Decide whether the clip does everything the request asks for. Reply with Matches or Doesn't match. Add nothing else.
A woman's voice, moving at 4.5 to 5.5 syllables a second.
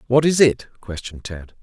Doesn't match